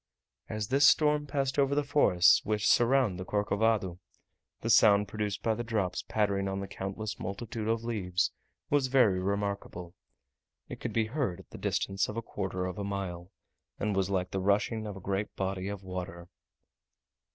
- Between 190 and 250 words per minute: No, average, 175 wpm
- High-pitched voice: No, low, 100 Hz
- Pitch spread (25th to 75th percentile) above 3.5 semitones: No, average, 3.0 semitones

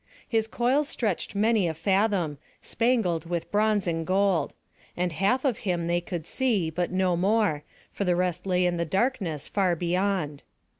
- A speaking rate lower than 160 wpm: No, average, 165 wpm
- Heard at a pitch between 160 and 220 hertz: Yes, medium, 185 Hz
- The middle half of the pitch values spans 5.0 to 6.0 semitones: No, average, 3.7 semitones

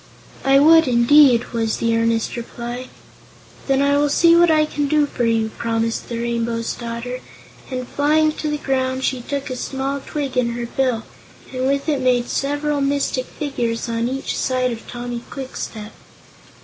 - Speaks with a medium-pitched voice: No, very high, 255 Hz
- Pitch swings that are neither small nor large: Yes, average, 3.2 semitones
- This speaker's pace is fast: No, average, 170 wpm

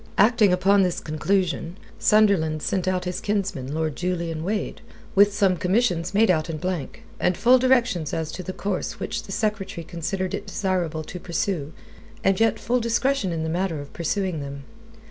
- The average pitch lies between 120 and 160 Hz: No, medium, 185 Hz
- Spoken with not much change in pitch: No, average, 3.7 semitones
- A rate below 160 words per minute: No, average, 175 wpm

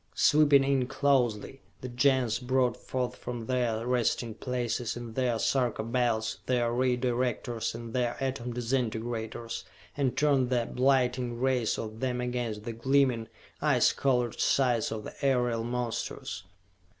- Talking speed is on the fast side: No, average, 140 wpm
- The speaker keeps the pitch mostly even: Yes, narrow, 1.9 semitones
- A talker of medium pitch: No, low, 125 Hz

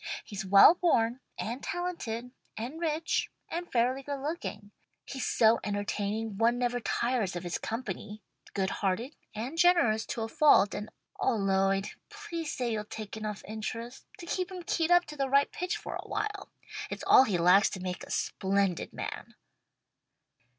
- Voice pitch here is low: No, high, 230 Hz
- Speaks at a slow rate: No, average, 165 wpm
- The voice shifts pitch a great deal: Yes, wide, 6.7 semitones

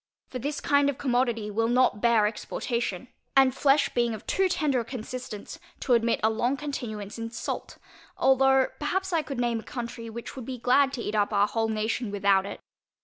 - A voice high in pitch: Yes, high, 240 Hz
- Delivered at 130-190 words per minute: No, average, 200 wpm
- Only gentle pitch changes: No, average, 3.4 semitones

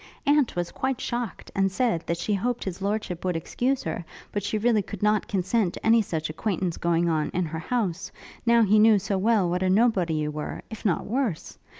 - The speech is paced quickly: Yes, fast, 215 wpm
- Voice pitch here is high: Yes, high, 195 Hz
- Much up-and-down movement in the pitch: No, average, 4.6 semitones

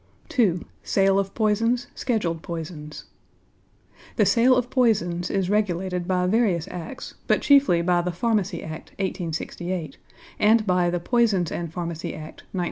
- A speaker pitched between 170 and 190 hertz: Yes, medium, 185 Hz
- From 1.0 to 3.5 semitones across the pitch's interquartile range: No, average, 4.0 semitones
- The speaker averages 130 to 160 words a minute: Yes, average, 140 wpm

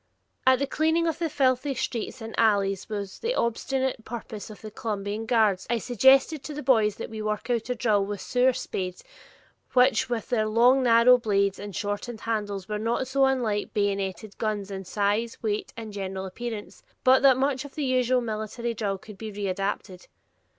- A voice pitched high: Yes, high, 225 Hz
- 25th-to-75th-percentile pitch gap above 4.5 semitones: No, average, 3.9 semitones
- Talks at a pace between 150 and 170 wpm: No, average, 185 wpm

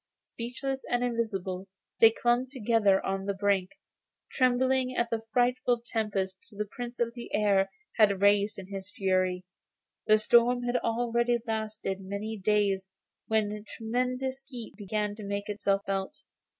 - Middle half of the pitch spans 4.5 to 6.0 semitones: No, average, 3.5 semitones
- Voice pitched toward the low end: No, high, 215 Hz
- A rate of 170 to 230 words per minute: No, average, 140 wpm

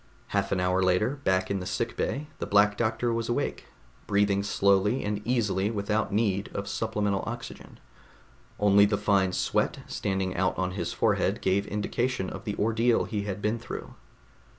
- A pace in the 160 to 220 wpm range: Yes, average, 165 wpm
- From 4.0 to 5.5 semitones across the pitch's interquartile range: No, narrow, 2.4 semitones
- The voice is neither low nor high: No, low, 100 Hz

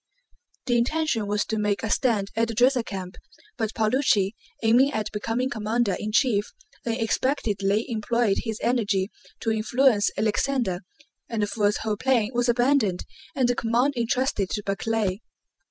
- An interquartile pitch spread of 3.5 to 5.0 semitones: No, average, 2.8 semitones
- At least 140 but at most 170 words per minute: Yes, average, 145 wpm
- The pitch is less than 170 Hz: No, high, 225 Hz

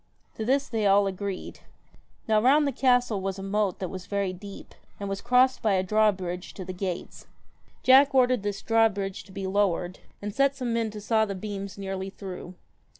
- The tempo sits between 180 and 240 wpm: Yes, average, 195 wpm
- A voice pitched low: No, high, 205 Hz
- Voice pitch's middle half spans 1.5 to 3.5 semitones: Yes, average, 3.0 semitones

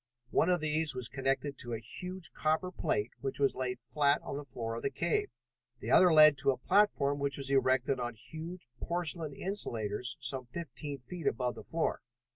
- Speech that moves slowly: No, average, 190 wpm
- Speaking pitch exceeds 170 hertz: No, medium, 140 Hz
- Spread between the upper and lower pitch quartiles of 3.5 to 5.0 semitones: Yes, average, 4.3 semitones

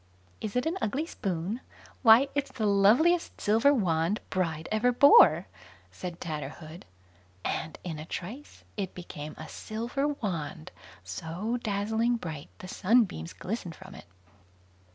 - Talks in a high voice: Yes, high, 200 Hz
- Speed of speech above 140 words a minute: No, slow, 135 wpm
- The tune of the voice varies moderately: No, wide, 6.4 semitones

